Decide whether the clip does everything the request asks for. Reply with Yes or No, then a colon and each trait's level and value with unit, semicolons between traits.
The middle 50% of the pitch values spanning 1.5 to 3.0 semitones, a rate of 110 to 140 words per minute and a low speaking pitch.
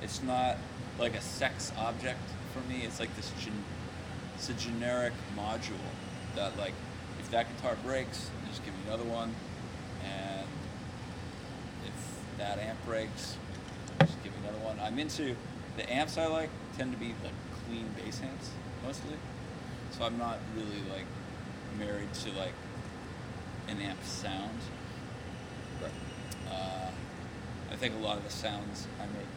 No: narrow, 2.6 semitones; average, 150 wpm; low, 110 Hz